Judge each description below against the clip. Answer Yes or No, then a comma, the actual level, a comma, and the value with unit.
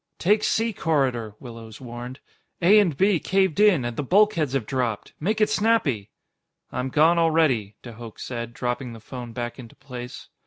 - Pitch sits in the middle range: No, low, 130 Hz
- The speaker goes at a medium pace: Yes, average, 170 wpm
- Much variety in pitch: Yes, wide, 6.5 semitones